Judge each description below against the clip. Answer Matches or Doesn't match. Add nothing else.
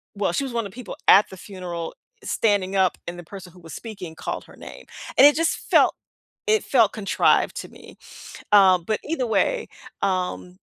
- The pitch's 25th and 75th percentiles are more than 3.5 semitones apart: Matches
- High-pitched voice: Matches